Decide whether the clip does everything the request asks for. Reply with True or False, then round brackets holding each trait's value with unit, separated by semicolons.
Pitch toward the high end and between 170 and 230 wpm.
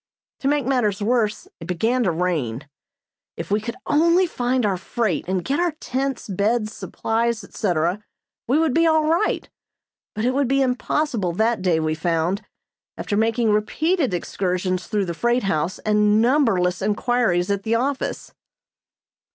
False (220 Hz; 155 wpm)